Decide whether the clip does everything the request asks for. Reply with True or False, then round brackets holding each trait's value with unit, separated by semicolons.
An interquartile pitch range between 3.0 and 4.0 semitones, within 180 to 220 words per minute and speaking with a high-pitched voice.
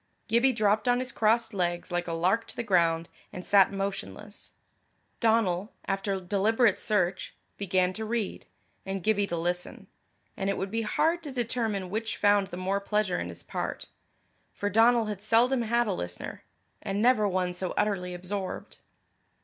False (3.4 semitones; 165 wpm; 200 Hz)